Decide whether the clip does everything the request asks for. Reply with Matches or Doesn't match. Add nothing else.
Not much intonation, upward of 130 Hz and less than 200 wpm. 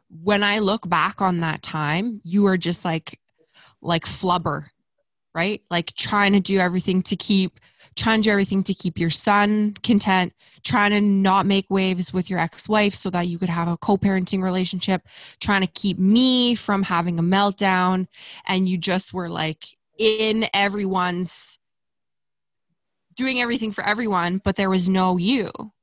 Matches